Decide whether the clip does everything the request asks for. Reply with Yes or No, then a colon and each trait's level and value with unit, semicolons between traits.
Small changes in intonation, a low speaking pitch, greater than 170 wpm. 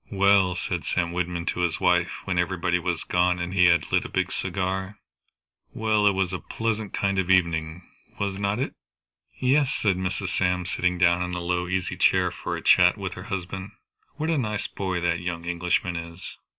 Yes: narrow, 1.8 semitones; very low, 90 Hz; average, 200 wpm